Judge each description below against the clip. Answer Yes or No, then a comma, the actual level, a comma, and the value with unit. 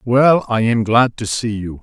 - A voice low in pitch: Yes, low, 115 Hz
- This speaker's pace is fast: Yes, fast, 230 wpm